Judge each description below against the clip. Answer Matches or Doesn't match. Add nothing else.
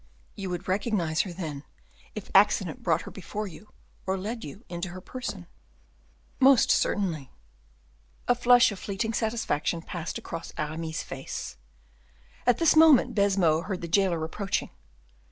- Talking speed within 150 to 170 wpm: Doesn't match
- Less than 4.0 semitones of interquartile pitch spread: Doesn't match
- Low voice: Doesn't match